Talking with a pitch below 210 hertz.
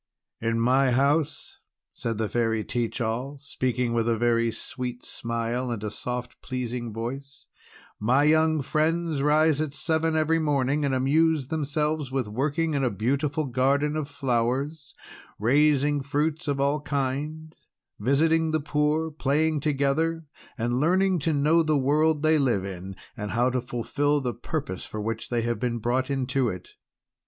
Yes: medium, 140 Hz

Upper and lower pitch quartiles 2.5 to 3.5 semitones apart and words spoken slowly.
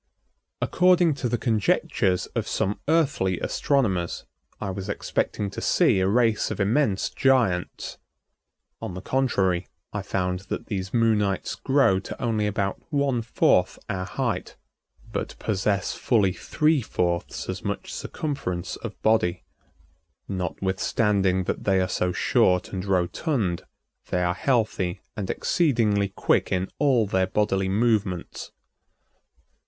No: average, 4.2 semitones; slow, 125 wpm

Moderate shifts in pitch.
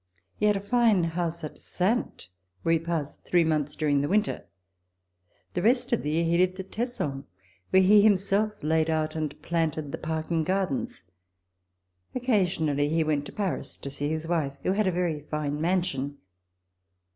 Yes: average, 4.0 semitones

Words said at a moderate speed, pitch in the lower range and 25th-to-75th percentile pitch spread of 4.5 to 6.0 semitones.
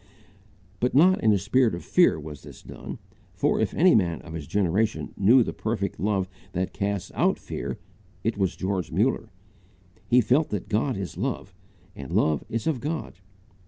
Yes: average, 175 wpm; low, 105 Hz; average, 5.1 semitones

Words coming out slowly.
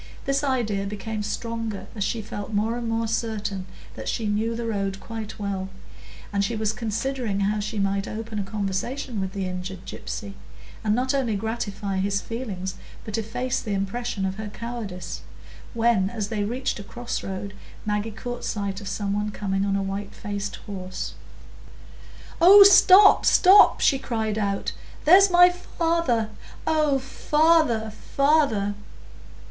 No: average, 155 wpm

